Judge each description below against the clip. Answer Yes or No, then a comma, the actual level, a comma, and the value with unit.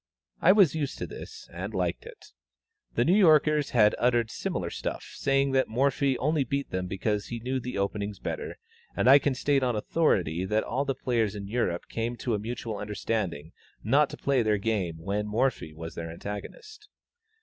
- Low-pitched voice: Yes, low, 115 Hz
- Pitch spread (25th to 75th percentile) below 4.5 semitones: No, average, 5.2 semitones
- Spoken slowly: No, average, 185 wpm